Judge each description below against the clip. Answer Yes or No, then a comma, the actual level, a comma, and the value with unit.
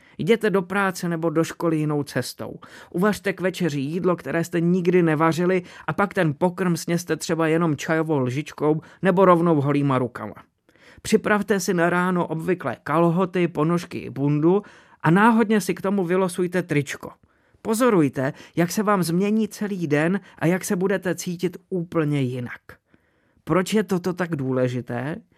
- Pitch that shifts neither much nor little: Yes, average, 3.6 semitones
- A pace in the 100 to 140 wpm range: No, average, 150 wpm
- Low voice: No, medium, 175 Hz